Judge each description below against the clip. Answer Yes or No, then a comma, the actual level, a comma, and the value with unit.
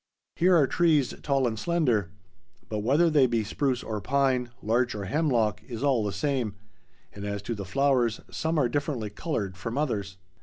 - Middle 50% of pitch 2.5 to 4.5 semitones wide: No, average, 5.1 semitones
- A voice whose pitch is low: Yes, low, 125 Hz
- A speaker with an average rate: Yes, average, 175 wpm